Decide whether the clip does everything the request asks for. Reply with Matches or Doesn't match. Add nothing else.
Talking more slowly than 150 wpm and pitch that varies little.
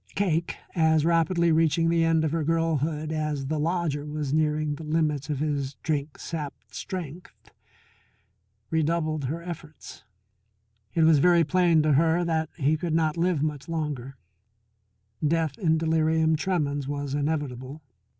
Matches